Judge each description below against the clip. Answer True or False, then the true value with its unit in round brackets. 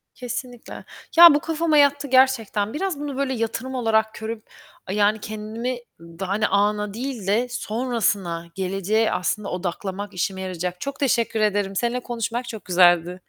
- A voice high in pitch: True (220 Hz)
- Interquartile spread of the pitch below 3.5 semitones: False (4.4 semitones)